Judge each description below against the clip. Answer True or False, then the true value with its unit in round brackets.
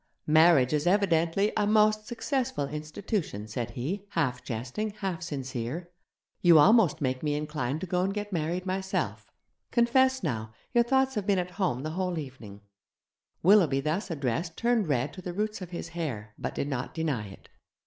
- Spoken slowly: False (170 wpm)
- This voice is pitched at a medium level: True (165 Hz)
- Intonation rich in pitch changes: True (6.5 semitones)